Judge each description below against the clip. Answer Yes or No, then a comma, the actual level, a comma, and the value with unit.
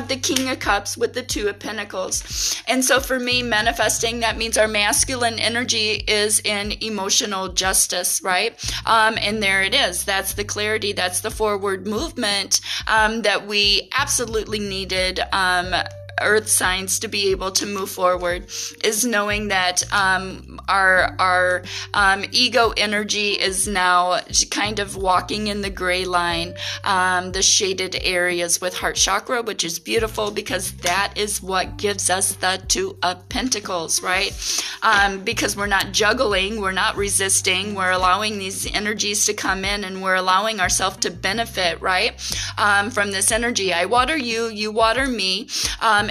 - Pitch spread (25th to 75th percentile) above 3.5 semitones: No, average, 2.8 semitones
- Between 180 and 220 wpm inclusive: No, average, 160 wpm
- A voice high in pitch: Yes, high, 205 Hz